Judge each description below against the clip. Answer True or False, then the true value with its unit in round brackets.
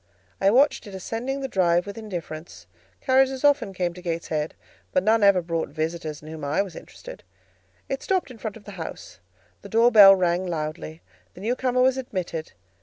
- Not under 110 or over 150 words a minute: False (185 wpm)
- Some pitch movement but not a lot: False (6.3 semitones)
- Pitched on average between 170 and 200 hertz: True (190 Hz)